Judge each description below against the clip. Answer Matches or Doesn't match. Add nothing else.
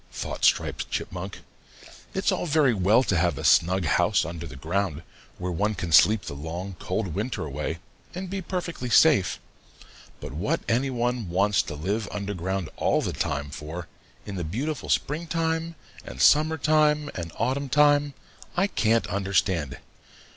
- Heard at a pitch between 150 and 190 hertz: Doesn't match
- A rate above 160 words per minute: Doesn't match